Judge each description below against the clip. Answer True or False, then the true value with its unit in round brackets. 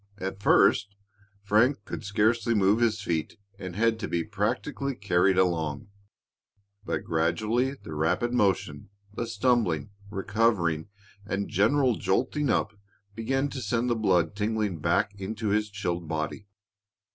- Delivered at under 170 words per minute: True (135 wpm)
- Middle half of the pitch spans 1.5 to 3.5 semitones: False (4.1 semitones)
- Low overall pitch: True (105 Hz)